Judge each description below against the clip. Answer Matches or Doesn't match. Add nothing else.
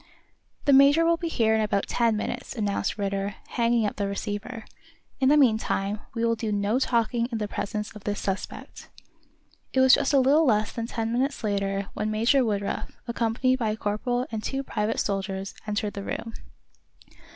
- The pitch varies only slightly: Doesn't match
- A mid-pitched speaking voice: Doesn't match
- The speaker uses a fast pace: Doesn't match